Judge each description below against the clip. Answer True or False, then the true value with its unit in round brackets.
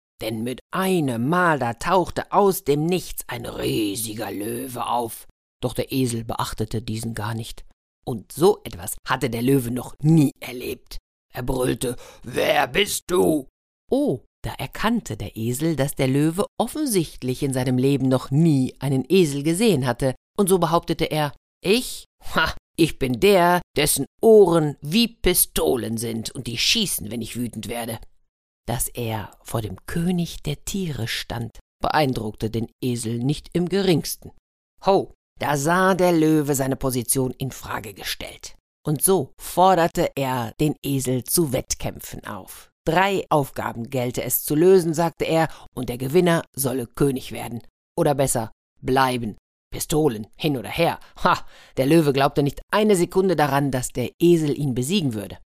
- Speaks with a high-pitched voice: False (135 Hz)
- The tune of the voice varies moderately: False (5.9 semitones)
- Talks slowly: False (155 wpm)